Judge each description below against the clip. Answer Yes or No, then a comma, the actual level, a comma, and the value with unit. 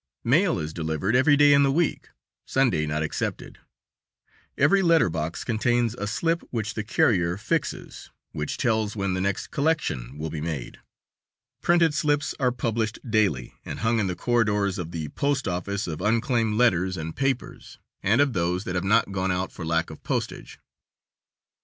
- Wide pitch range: Yes, wide, 6.5 semitones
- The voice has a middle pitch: No, low, 105 Hz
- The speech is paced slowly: No, average, 170 wpm